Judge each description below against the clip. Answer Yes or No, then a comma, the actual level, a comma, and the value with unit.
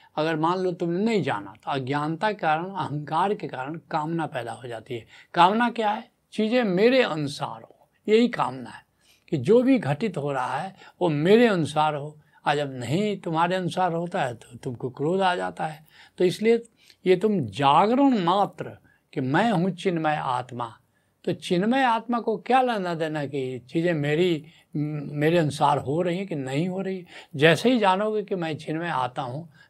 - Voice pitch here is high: No, medium, 165 Hz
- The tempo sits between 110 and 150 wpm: No, average, 185 wpm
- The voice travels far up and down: No, average, 4.8 semitones